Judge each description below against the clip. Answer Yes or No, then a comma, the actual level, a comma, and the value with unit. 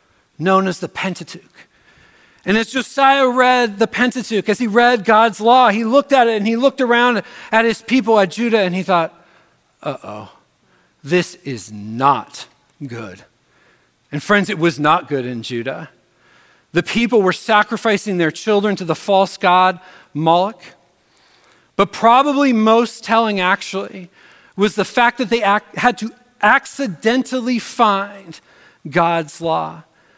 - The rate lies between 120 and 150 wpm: Yes, average, 145 wpm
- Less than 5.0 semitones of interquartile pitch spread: No, average, 5.3 semitones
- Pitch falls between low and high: No, high, 210 Hz